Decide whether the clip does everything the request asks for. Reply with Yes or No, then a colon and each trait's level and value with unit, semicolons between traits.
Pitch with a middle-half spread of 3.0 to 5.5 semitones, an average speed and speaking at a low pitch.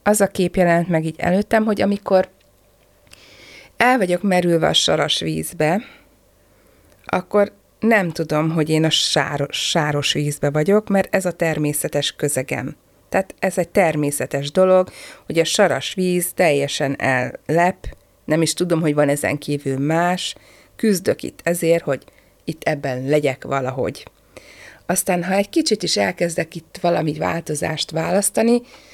No: average, 4.4 semitones; average, 140 wpm; medium, 170 Hz